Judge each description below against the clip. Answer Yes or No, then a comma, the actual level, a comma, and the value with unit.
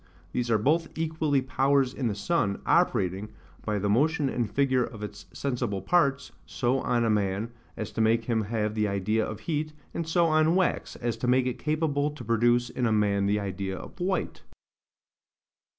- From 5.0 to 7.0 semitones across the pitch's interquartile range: Yes, wide, 5.4 semitones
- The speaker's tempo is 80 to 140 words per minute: No, average, 185 wpm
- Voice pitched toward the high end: No, low, 120 Hz